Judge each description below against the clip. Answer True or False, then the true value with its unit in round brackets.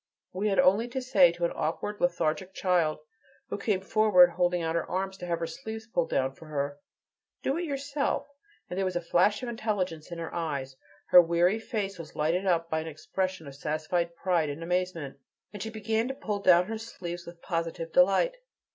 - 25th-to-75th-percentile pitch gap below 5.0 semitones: True (3.8 semitones)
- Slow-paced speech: False (200 wpm)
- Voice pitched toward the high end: False (180 Hz)